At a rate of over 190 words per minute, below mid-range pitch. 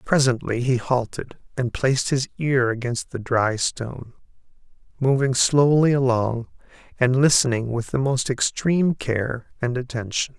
No: slow, 135 wpm; low, 125 Hz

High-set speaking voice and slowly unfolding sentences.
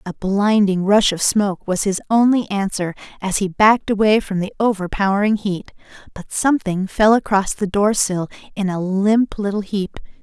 No: high, 200 Hz; average, 170 wpm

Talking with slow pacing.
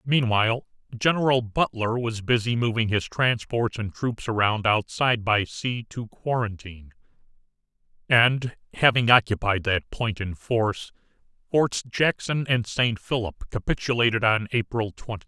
Yes: slow, 130 wpm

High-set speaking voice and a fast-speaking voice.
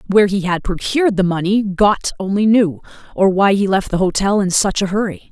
Yes: high, 195 Hz; fast, 215 wpm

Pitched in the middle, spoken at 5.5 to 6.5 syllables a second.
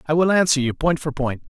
Yes: medium, 150 Hz; 6.0 syllables/s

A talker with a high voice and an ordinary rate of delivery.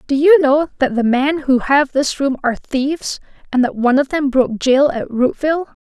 No: very high, 275 Hz; fast, 215 wpm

